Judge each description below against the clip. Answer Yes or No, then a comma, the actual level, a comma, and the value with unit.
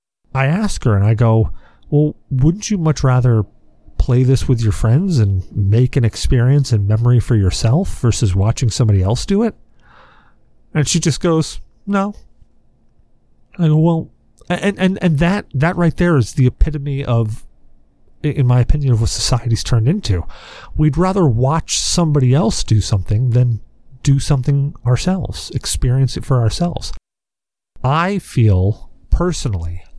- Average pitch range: No, wide, 5.9 semitones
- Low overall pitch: Yes, low, 130 Hz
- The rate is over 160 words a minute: No, average, 150 wpm